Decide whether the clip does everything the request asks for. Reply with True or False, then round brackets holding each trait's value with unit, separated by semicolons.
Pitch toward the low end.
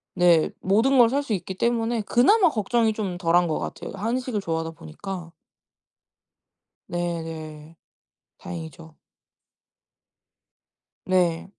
False (185 Hz)